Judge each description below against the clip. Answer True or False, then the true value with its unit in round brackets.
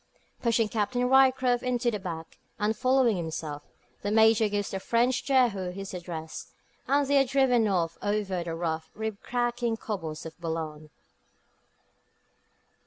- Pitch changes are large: True (6.0 semitones)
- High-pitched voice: True (210 Hz)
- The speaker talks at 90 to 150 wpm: True (140 wpm)